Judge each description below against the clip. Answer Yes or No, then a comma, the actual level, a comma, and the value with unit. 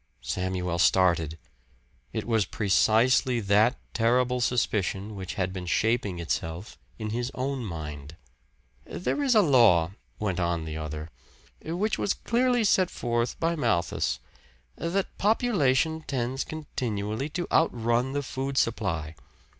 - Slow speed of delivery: Yes, slow, 125 wpm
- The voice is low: Yes, low, 115 Hz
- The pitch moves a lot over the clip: Yes, wide, 6.9 semitones